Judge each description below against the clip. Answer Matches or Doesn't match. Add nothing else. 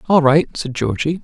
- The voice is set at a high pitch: Doesn't match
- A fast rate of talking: Doesn't match